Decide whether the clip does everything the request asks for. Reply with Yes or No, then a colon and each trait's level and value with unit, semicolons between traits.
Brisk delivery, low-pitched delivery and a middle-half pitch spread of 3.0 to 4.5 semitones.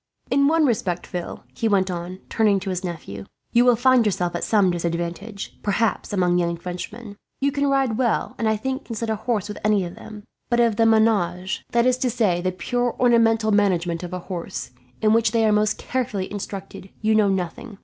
No: fast, 210 wpm; high, 210 Hz; average, 4.2 semitones